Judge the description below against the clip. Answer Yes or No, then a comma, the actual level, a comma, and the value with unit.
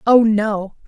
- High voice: Yes, high, 215 Hz